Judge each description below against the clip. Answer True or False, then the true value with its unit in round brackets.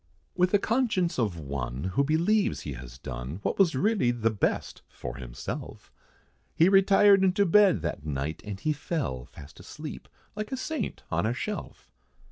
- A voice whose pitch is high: False (140 Hz)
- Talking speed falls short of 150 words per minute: False (165 wpm)